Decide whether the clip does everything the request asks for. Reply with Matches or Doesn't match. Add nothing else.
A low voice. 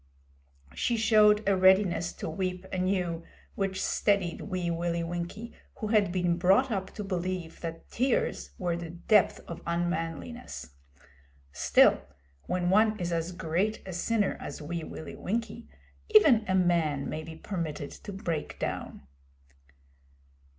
Doesn't match